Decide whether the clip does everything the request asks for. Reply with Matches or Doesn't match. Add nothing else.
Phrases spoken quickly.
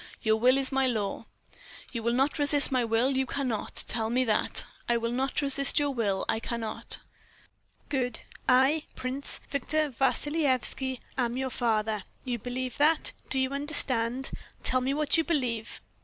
Doesn't match